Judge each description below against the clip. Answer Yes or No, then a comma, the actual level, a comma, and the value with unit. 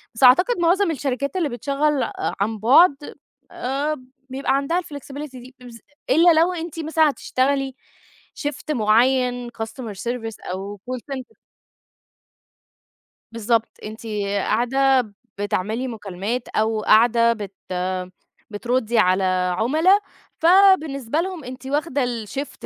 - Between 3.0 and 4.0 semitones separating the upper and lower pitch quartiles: No, average, 4.7 semitones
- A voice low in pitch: No, very high, 255 Hz